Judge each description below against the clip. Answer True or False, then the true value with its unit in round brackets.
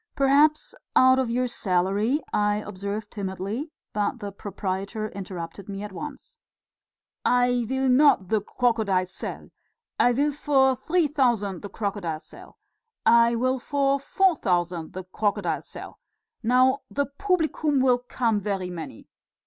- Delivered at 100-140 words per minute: True (135 wpm)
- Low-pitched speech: False (230 Hz)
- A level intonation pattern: False (5.1 semitones)